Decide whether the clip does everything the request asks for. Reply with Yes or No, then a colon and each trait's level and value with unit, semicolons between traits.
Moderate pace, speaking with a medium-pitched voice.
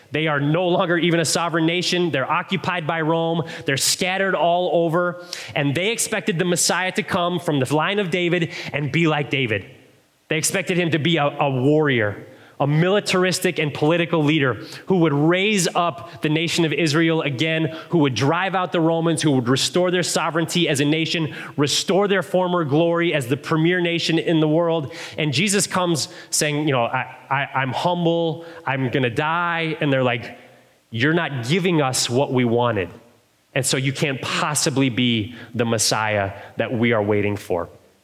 Yes: average, 185 wpm; medium, 160 Hz